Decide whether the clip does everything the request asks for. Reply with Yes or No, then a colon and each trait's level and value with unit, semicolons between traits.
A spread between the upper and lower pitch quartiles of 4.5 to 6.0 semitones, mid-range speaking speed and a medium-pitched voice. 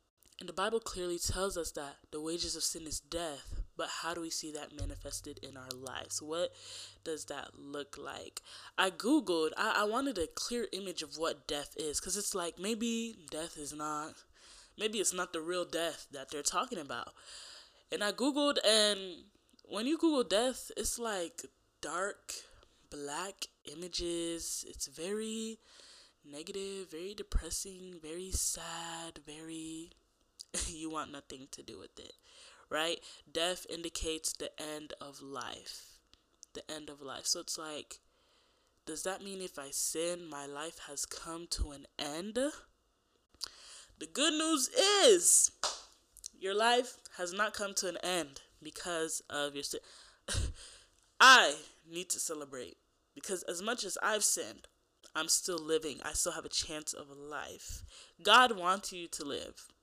Yes: average, 5.1 semitones; average, 155 wpm; medium, 170 Hz